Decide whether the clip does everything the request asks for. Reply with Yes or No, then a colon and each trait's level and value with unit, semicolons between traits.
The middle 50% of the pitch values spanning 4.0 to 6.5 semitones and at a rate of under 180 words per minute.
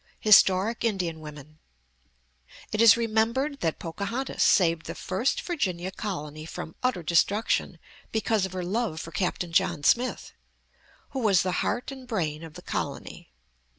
Yes: wide, 5.6 semitones; average, 145 wpm